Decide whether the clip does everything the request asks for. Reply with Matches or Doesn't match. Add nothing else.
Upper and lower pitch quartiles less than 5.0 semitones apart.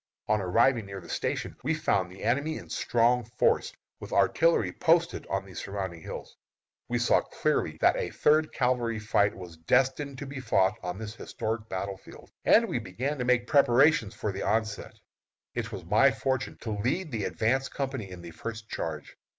Doesn't match